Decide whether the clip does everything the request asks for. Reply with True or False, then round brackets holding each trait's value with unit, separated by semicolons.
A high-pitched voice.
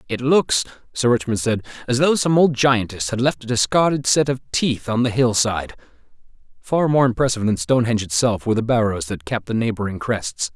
False (120 Hz)